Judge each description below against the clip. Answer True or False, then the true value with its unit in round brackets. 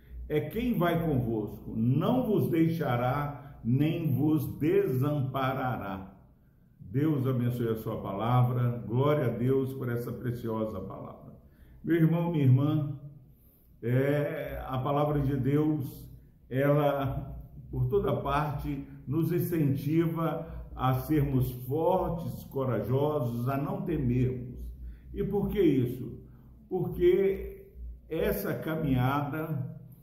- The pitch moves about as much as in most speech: True (3.8 semitones)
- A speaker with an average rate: False (100 wpm)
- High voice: False (140 Hz)